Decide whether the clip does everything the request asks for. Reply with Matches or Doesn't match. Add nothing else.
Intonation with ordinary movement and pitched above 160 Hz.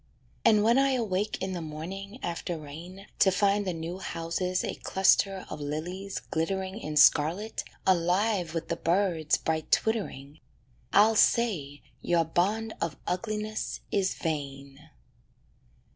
Matches